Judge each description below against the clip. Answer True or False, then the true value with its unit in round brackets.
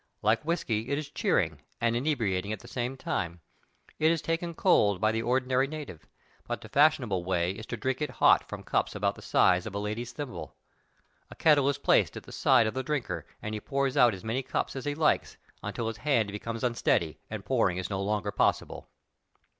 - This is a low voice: True (120 Hz)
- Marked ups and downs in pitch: False (4.9 semitones)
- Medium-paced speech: False (210 wpm)